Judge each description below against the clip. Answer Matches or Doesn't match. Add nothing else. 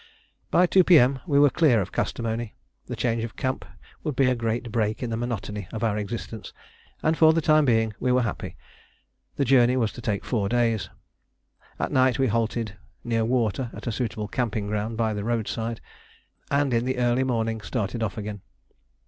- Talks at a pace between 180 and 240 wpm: Matches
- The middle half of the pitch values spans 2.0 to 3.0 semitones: Matches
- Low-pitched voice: Matches